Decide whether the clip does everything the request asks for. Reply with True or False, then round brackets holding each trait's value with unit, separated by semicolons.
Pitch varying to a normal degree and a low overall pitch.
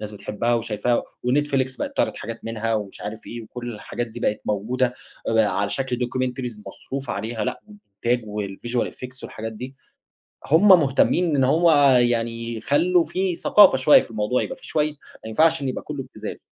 True (3.6 semitones; 120 Hz)